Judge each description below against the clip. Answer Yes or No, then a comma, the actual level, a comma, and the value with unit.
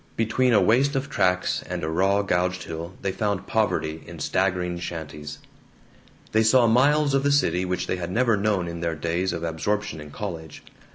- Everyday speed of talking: Yes, average, 185 wpm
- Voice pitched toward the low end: Yes, very low, 95 Hz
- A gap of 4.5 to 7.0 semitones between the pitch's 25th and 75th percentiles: Yes, average, 4.8 semitones